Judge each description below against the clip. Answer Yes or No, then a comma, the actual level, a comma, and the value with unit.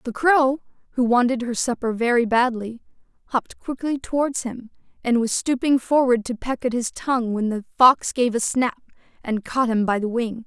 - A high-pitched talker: Yes, high, 245 Hz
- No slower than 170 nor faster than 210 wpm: Yes, average, 190 wpm